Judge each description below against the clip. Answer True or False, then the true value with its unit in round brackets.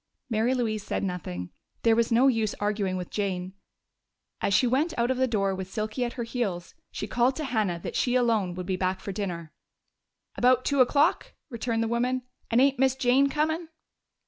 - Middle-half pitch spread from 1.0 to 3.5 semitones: False (4.6 semitones)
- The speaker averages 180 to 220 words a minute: True (195 wpm)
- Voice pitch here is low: False (230 Hz)